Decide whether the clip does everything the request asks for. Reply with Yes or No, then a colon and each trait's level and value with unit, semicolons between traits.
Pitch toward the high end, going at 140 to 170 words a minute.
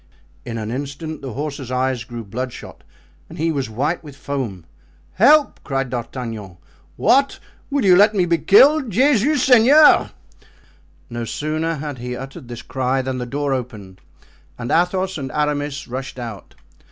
No: low, 135 Hz; average, 155 wpm